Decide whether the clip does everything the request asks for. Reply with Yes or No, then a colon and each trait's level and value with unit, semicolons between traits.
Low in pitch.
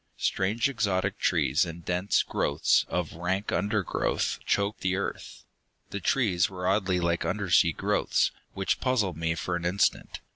Yes: very low, 95 Hz